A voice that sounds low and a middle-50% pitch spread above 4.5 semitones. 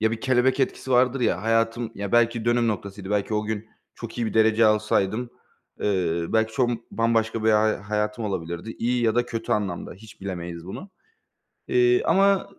No: low, 110 Hz; narrow, 2.5 semitones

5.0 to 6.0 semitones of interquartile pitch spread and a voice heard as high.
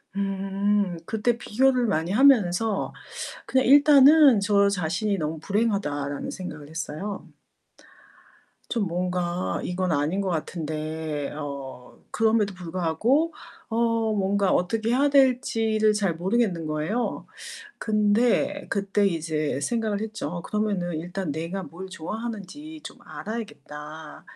Yes: average, 5.3 semitones; high, 195 Hz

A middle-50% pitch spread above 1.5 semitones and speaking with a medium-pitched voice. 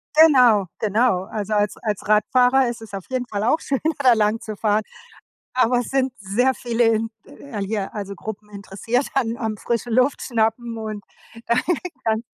No: average, 2.8 semitones; high, 225 Hz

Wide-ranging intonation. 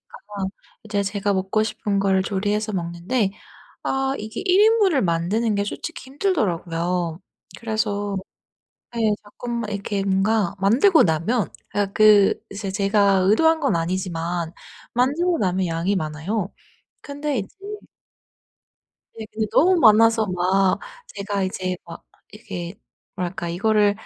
No: average, 3.3 semitones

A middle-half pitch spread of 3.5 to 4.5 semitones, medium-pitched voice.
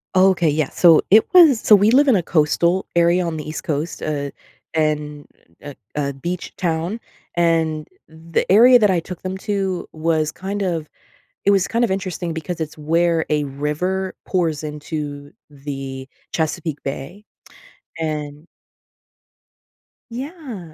Yes: average, 4.0 semitones; medium, 165 Hz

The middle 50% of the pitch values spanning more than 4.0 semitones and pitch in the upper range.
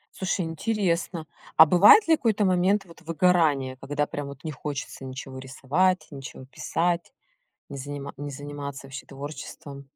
No: average, 4.6 semitones; medium, 145 Hz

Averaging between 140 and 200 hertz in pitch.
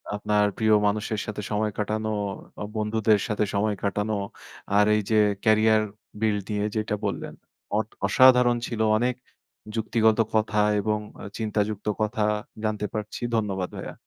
No: low, 110 Hz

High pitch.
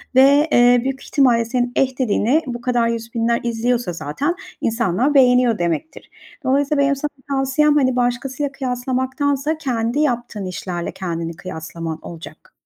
Yes: high, 245 Hz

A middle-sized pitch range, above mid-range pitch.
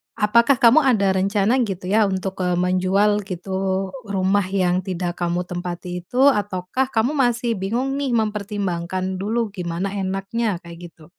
Yes: average, 3.1 semitones; high, 195 Hz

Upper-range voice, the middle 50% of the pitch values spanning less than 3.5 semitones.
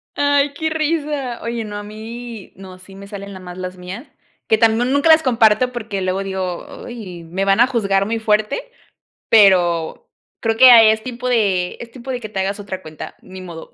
No: high, 215 Hz; average, 4.3 semitones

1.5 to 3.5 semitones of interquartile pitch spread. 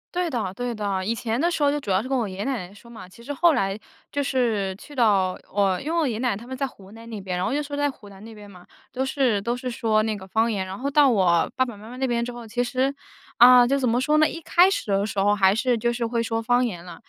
No: average, 4.4 semitones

